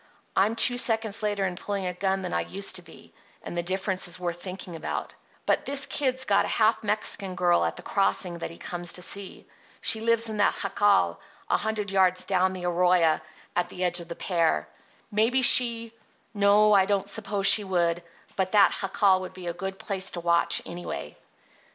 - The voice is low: No, high, 190 Hz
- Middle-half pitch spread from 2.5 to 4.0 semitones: Yes, average, 2.9 semitones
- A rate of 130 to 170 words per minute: No, average, 195 wpm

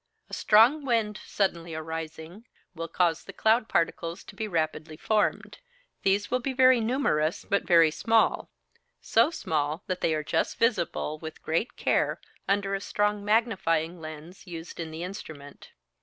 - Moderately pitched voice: Yes, medium, 180 Hz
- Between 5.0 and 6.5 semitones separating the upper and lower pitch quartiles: Yes, average, 5.3 semitones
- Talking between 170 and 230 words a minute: No, average, 155 wpm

